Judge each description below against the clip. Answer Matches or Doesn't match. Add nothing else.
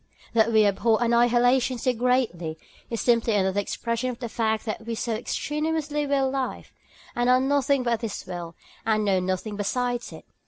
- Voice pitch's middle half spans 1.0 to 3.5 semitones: Matches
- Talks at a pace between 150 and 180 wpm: Matches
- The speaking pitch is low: Doesn't match